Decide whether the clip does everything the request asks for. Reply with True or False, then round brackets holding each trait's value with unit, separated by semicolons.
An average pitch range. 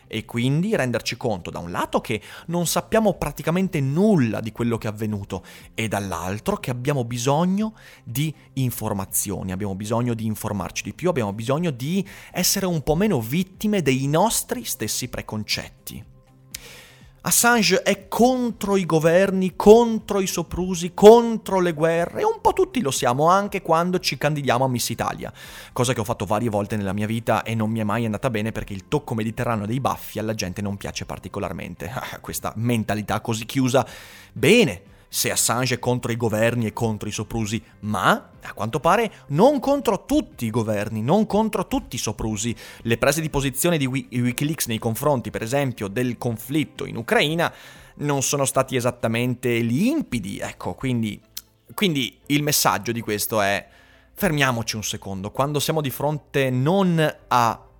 False (7.6 semitones)